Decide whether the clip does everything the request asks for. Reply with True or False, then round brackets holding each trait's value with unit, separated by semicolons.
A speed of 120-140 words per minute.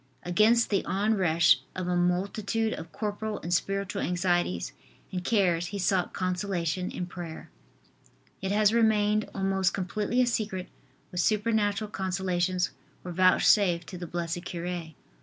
True (135 wpm)